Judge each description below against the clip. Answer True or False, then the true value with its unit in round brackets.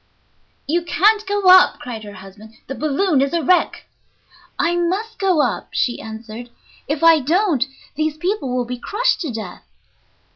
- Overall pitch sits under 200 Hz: False (305 Hz)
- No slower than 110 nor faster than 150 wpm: False (160 wpm)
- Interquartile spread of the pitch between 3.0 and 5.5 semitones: False (7.0 semitones)